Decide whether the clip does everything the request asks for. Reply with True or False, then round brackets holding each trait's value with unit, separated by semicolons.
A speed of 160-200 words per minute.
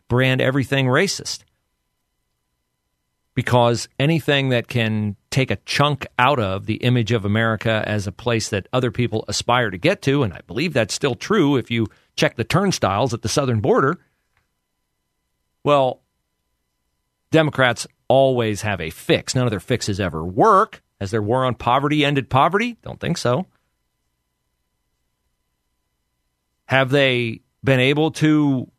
False (140 wpm)